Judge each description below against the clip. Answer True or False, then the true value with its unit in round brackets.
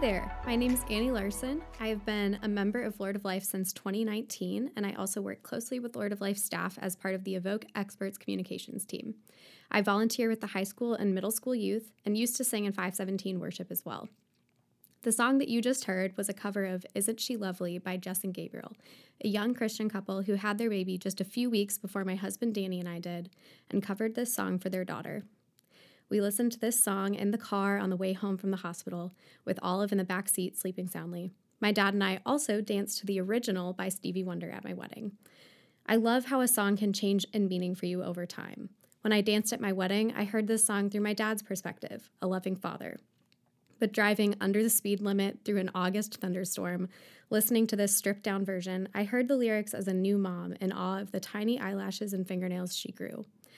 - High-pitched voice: True (200 Hz)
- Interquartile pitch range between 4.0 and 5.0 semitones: False (2.5 semitones)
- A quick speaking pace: True (225 wpm)